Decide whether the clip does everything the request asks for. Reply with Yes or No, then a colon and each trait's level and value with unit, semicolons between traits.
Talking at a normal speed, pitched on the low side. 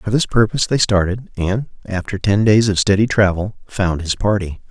Yes: average, 190 wpm; low, 100 Hz